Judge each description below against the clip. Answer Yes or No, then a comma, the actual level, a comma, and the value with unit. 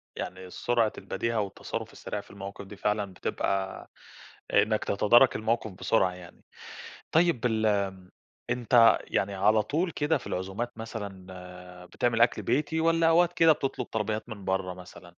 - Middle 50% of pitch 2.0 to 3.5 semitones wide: No, average, 4.0 semitones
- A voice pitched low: Yes, low, 110 Hz